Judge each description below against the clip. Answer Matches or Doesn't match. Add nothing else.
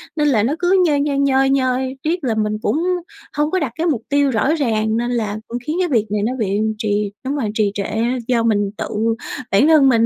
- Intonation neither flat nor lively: Matches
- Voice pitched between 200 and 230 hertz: Doesn't match